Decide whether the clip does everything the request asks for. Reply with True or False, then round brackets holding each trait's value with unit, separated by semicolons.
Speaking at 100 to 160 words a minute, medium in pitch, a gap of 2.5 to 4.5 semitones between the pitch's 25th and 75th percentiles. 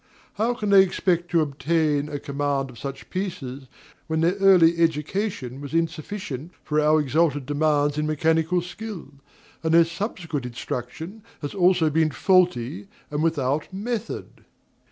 True (140 wpm; 160 Hz; 3.7 semitones)